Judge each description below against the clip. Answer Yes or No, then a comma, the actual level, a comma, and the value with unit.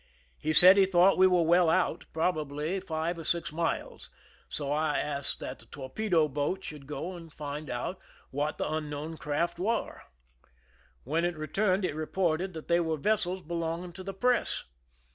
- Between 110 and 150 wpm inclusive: No, average, 175 wpm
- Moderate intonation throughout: Yes, average, 3.3 semitones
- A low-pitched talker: No, medium, 165 Hz